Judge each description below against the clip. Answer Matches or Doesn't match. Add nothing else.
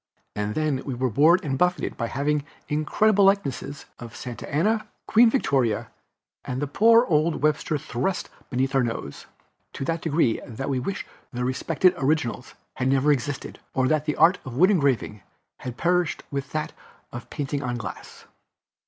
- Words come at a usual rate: Matches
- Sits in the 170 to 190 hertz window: Doesn't match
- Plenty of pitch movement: Doesn't match